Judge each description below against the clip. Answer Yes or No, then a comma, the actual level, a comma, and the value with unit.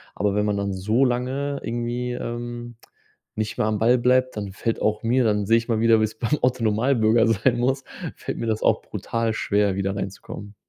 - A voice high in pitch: No, low, 115 Hz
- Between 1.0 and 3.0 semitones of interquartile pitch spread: Yes, average, 2.7 semitones